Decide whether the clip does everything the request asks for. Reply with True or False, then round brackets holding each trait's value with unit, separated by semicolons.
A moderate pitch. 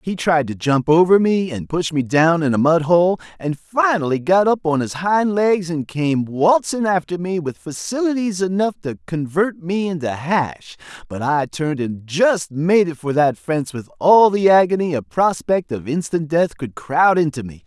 True (165 Hz)